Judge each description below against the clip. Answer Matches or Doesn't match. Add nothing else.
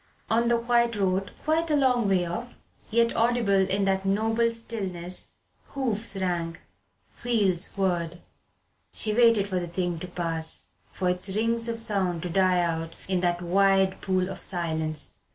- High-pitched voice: Matches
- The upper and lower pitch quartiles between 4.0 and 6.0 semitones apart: Matches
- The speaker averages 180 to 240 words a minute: Doesn't match